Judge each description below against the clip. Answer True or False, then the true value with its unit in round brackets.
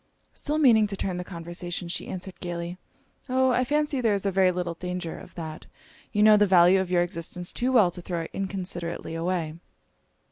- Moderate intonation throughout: True (3.2 semitones)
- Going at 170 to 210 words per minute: True (190 wpm)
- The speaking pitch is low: False (180 Hz)